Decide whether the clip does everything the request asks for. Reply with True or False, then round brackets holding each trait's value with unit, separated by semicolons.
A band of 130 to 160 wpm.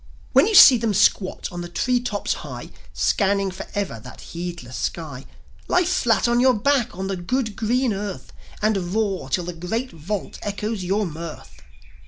False (175 wpm)